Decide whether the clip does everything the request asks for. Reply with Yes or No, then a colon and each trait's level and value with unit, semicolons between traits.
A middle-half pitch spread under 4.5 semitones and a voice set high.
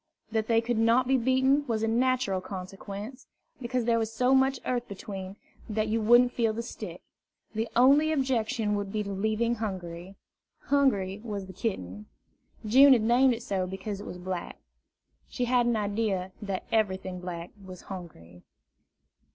Yes: average, 4.1 semitones; high, 220 Hz